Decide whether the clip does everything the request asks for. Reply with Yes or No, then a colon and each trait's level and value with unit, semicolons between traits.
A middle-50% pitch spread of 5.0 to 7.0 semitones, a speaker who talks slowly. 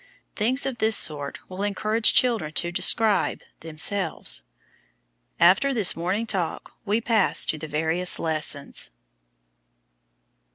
Yes: wide, 5.4 semitones; slow, 115 wpm